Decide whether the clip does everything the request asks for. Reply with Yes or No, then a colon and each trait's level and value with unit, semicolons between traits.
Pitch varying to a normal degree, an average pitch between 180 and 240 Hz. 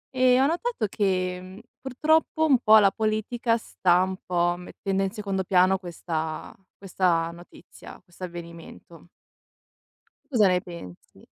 Yes: average, 3.9 semitones; high, 190 Hz